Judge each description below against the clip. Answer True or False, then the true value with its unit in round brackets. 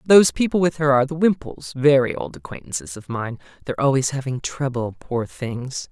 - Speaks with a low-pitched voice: True (130 Hz)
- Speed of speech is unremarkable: True (185 wpm)